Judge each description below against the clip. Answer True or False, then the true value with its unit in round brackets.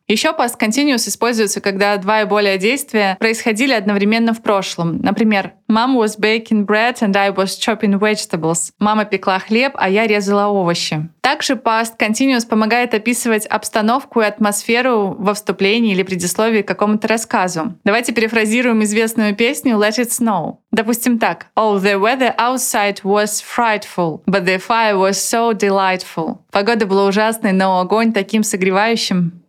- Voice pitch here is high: True (215 Hz)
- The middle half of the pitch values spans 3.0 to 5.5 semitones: False (2.4 semitones)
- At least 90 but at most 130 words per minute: False (150 wpm)